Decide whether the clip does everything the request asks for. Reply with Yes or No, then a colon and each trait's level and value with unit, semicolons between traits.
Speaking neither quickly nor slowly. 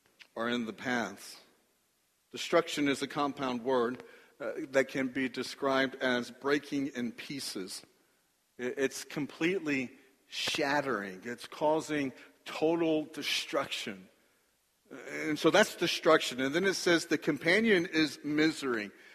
No: slow, 115 wpm